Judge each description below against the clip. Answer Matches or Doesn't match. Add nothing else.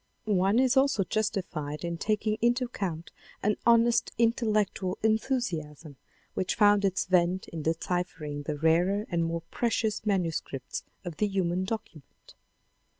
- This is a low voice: Doesn't match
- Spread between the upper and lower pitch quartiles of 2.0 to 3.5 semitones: Doesn't match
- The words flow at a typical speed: Doesn't match